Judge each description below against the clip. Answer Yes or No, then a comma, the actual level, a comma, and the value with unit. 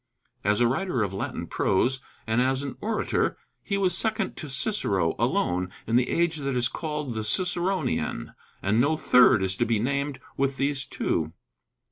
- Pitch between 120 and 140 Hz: Yes, low, 135 Hz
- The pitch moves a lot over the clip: Yes, wide, 6.4 semitones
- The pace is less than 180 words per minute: Yes, average, 170 wpm